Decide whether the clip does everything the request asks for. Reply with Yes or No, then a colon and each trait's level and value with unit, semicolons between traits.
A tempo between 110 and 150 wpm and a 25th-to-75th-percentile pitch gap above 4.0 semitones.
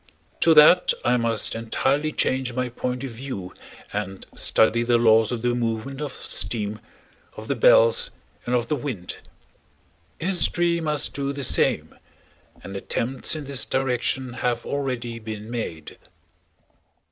No: average, 140 wpm; average, 3.7 semitones